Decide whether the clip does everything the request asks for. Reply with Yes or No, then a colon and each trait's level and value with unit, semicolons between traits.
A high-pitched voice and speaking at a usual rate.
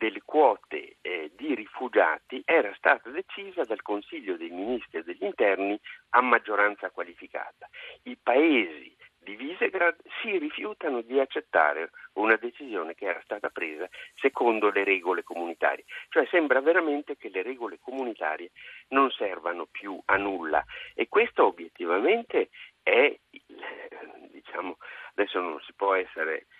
Yes: very high, 360 Hz; average, 135 wpm